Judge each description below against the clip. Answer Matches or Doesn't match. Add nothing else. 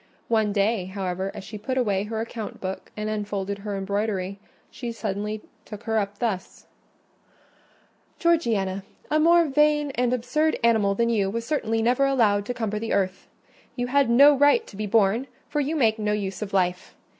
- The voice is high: Matches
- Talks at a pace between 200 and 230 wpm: Doesn't match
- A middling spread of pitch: Matches